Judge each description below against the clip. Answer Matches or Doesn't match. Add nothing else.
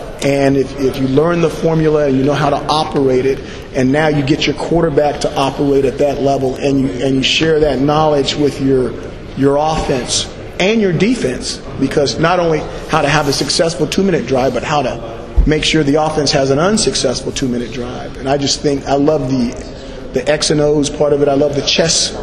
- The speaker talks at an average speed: Doesn't match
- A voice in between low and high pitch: Matches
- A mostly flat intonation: Matches